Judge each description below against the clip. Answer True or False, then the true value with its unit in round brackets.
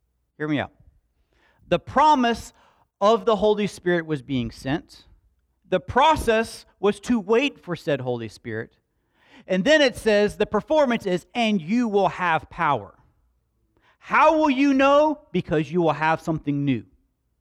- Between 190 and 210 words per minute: False (150 wpm)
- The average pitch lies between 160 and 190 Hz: True (185 Hz)